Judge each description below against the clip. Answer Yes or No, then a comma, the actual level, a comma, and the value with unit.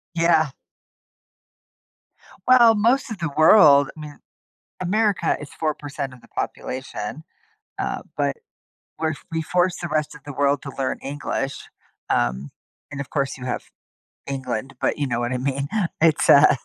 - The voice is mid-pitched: Yes, medium, 145 Hz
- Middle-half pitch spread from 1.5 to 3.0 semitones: No, average, 3.6 semitones